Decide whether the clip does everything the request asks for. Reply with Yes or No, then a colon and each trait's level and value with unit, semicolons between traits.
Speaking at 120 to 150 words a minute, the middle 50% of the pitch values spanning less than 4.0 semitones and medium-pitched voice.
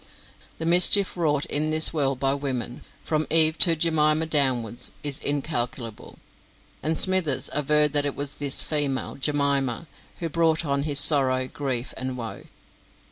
Yes: average, 145 wpm; average, 2.7 semitones; medium, 145 Hz